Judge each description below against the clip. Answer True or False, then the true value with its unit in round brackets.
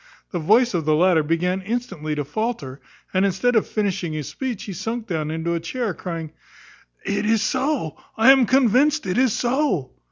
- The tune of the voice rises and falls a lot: True (6.7 semitones)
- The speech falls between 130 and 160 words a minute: False (185 wpm)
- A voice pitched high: True (195 Hz)